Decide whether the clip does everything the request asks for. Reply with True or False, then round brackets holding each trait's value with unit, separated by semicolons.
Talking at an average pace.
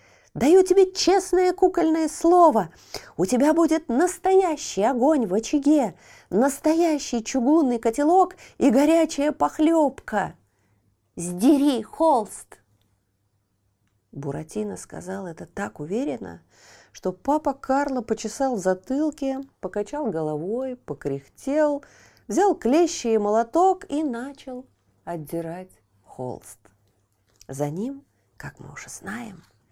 False (95 wpm)